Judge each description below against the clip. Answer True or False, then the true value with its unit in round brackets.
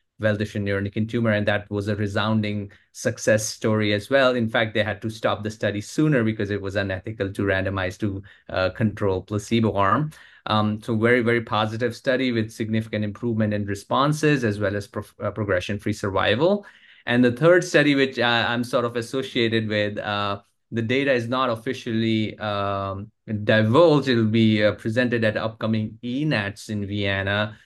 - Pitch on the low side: True (110 Hz)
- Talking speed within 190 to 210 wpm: False (170 wpm)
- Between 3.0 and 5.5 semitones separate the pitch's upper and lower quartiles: False (2.4 semitones)